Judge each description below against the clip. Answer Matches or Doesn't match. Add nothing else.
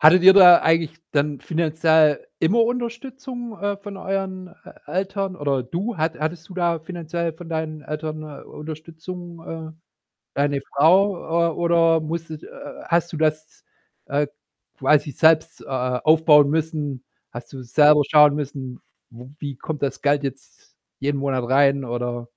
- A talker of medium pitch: Matches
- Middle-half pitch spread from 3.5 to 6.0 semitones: Doesn't match